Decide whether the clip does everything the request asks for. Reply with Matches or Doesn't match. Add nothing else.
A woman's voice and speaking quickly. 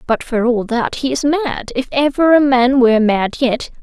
Matches